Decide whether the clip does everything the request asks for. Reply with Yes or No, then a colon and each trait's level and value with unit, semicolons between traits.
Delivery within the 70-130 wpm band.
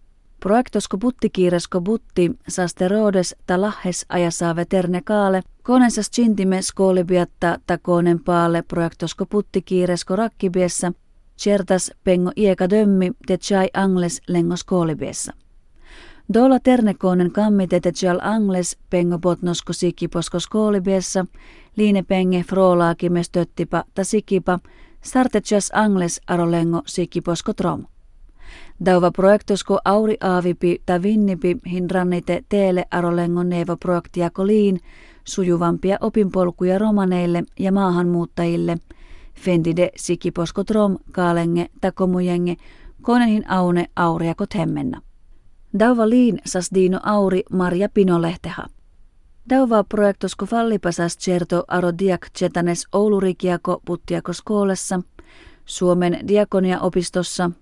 Yes: slow, 95 wpm